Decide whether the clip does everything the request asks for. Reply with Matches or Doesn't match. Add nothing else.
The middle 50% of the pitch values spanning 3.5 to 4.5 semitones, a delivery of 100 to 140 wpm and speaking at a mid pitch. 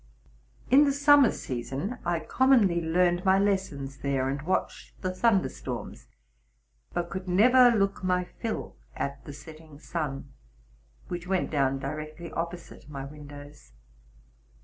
Doesn't match